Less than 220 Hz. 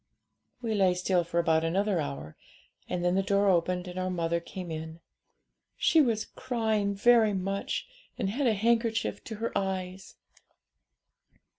Yes: high, 190 Hz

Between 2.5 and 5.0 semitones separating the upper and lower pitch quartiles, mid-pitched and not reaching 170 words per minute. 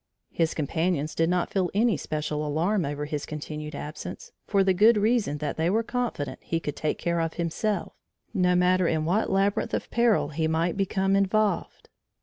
No: average, 4.3 semitones; medium, 175 Hz; average, 180 wpm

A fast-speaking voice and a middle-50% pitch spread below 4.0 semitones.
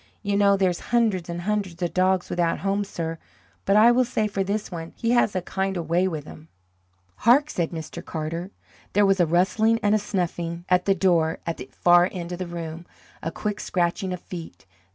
Yes: fast, 215 wpm; average, 2.9 semitones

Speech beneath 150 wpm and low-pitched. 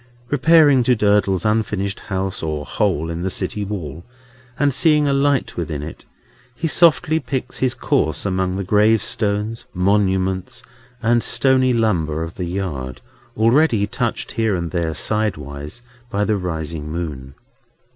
Yes: average, 140 wpm; low, 100 Hz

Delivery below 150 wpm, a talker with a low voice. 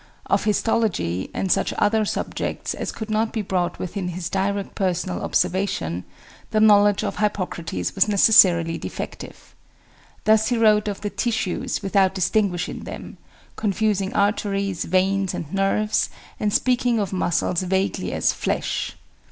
No: slow, 135 wpm; high, 195 Hz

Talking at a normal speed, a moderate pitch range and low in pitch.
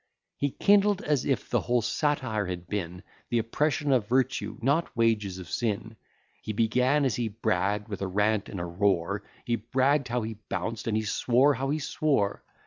Yes: average, 185 wpm; average, 4.7 semitones; low, 115 Hz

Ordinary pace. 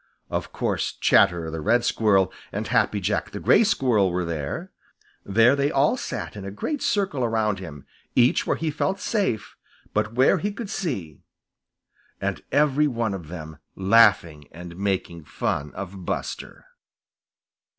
Yes: average, 150 wpm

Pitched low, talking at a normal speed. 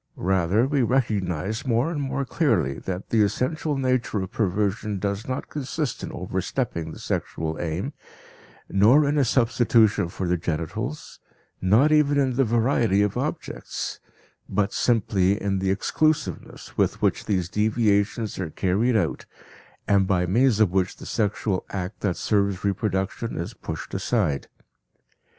Yes: low, 105 Hz; average, 145 wpm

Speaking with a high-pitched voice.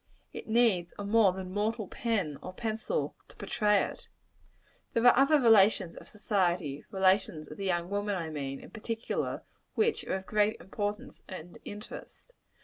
Yes: high, 205 Hz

